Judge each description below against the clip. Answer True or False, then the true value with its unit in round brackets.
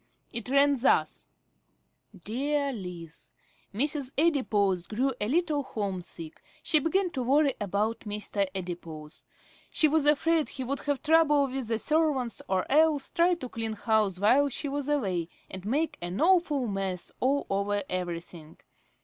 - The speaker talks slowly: False (150 wpm)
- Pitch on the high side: True (255 Hz)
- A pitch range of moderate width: False (6.8 semitones)